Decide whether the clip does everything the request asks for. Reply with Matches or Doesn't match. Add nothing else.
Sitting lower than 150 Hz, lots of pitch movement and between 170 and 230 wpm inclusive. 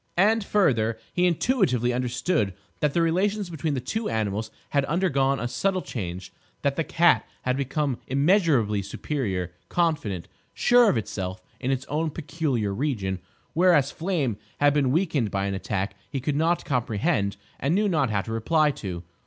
Doesn't match